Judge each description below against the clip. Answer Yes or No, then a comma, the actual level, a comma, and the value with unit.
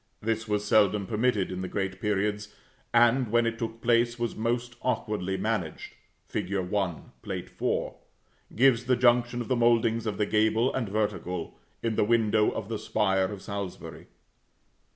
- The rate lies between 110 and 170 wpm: Yes, average, 160 wpm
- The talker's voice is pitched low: Yes, low, 110 Hz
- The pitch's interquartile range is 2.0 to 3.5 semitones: Yes, narrow, 2.6 semitones